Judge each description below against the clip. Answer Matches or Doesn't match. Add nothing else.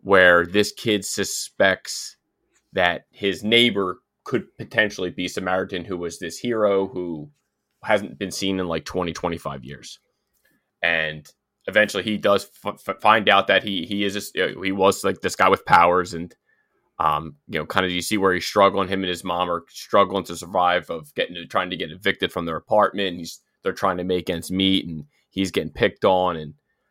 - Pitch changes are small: Matches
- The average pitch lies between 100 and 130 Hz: Doesn't match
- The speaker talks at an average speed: Matches